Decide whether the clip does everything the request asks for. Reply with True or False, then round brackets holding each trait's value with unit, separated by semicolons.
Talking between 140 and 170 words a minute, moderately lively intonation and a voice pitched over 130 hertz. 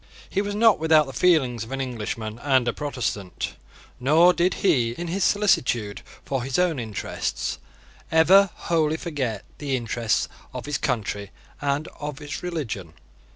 False (155 wpm; 6.1 semitones; 140 Hz)